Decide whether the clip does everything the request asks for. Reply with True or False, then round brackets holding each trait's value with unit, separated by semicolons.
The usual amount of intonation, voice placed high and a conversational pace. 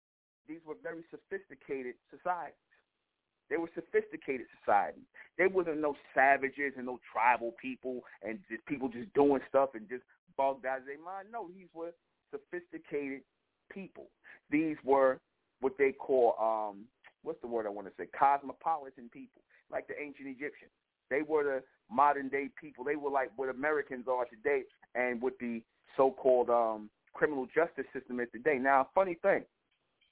False (4.1 semitones; 140 Hz; 160 wpm)